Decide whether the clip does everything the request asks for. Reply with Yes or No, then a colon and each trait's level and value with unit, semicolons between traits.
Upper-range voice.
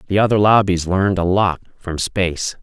No: very low, 95 Hz